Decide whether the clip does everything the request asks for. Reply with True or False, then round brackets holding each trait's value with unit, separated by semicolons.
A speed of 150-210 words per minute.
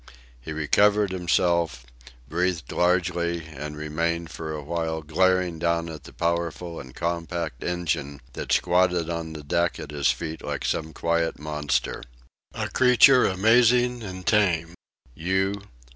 False (135 wpm)